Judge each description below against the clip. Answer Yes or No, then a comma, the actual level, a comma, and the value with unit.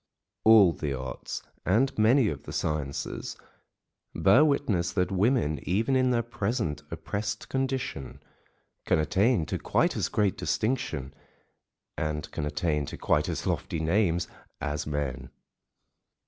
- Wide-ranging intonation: Yes, wide, 7.7 semitones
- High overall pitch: No, very low, 95 Hz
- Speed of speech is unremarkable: No, slow, 130 wpm